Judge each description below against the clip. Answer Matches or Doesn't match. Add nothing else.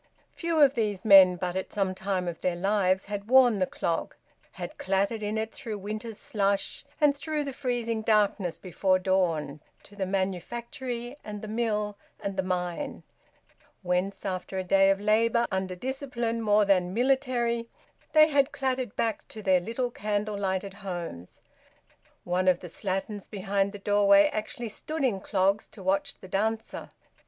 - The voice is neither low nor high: Doesn't match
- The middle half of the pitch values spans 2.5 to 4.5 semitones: Matches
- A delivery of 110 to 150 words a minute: Doesn't match